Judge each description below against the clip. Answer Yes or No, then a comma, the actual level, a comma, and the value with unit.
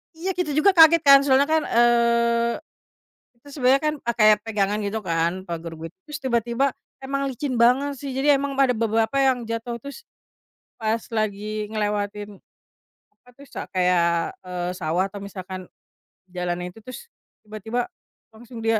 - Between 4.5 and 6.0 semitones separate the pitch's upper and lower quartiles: Yes, average, 4.8 semitones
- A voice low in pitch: No, high, 230 Hz